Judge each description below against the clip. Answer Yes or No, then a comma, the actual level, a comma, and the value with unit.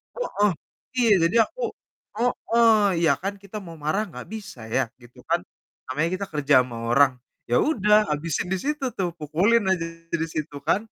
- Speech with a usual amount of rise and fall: No, wide, 6.4 semitones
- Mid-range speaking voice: Yes, medium, 180 Hz